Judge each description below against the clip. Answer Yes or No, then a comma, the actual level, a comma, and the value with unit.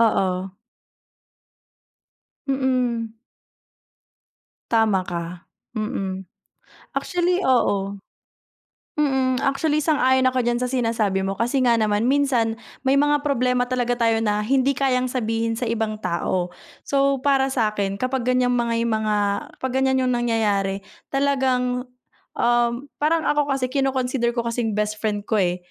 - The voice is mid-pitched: No, high, 240 Hz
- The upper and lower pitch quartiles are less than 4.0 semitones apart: Yes, average, 3.6 semitones